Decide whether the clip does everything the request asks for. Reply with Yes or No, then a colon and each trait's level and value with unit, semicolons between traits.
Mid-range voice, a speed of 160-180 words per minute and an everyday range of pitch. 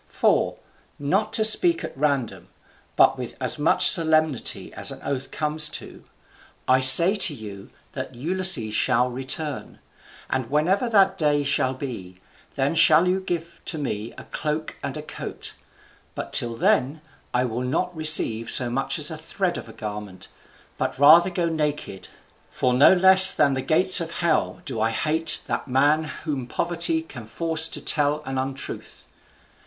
Yes: medium, 150 Hz; average, 165 wpm; average, 4.5 semitones